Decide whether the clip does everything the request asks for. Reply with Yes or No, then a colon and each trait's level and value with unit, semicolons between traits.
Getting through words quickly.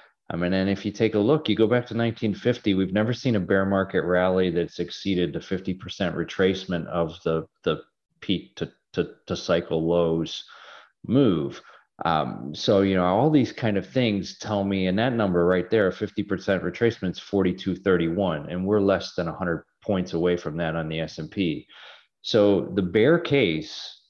No: average, 180 wpm